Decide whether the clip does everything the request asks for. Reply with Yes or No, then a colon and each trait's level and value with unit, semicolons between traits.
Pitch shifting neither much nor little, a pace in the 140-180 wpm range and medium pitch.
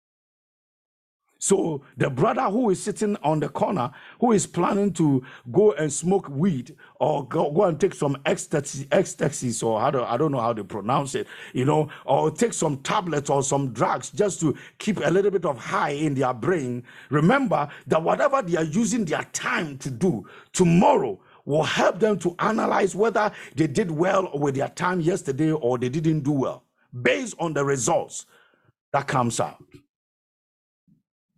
No: wide, 5.8 semitones; average, 175 wpm; medium, 165 Hz